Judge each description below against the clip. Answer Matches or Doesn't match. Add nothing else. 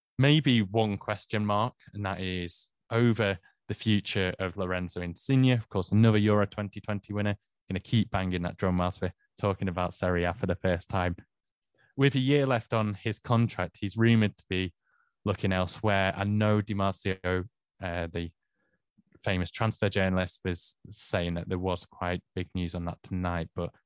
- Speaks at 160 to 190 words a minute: Matches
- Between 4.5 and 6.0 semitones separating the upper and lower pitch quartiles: Doesn't match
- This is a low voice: Matches